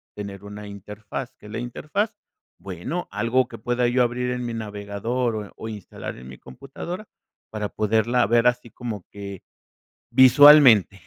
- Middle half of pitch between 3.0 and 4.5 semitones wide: Yes, average, 3.4 semitones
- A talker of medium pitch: No, low, 115 Hz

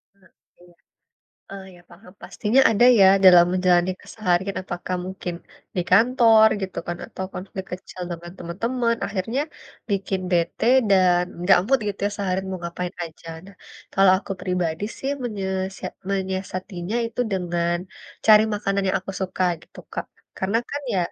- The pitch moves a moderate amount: No, narrow, 2.1 semitones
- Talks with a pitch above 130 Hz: Yes, high, 190 Hz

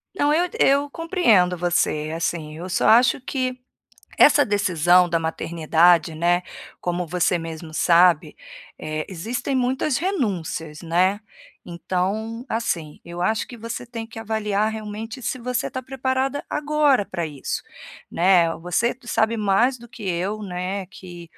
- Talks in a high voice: Yes, high, 195 Hz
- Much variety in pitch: Yes, wide, 5.9 semitones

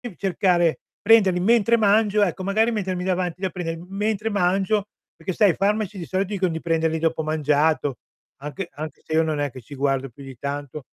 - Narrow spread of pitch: No, average, 4.2 semitones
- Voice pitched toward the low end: No, medium, 180 Hz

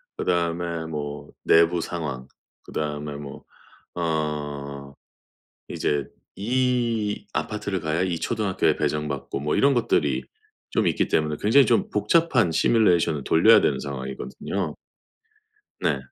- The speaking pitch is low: Yes, very low, 80 Hz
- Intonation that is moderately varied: No, wide, 5.9 semitones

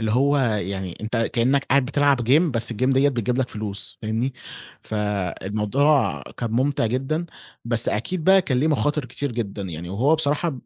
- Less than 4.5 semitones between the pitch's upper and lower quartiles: No, average, 4.8 semitones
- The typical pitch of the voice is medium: No, low, 125 Hz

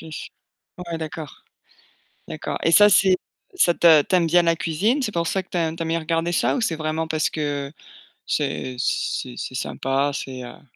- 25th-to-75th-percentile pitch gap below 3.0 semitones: Yes, narrow, 2.4 semitones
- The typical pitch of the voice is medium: Yes, medium, 165 Hz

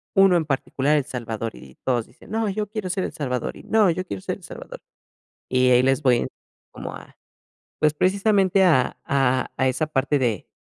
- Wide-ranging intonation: Yes, wide, 6.8 semitones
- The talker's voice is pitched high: No, medium, 145 Hz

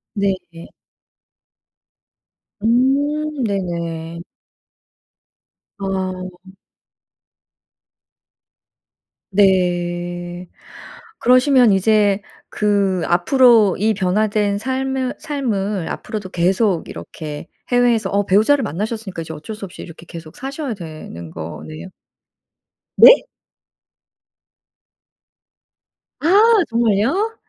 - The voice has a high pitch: Yes, high, 200 Hz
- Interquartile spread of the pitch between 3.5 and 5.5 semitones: Yes, average, 5.1 semitones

